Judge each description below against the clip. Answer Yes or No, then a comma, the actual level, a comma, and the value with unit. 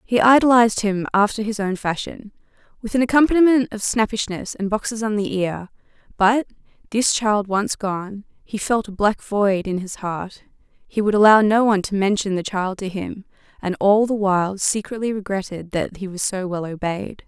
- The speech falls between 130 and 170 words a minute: No, average, 185 wpm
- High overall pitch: Yes, high, 205 Hz